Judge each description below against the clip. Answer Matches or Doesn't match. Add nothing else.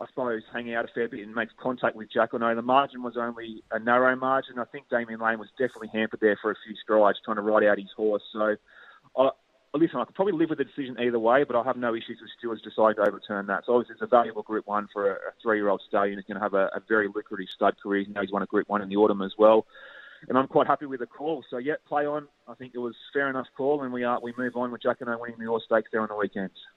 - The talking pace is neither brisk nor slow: Doesn't match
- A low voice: Matches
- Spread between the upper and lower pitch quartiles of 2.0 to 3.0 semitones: Matches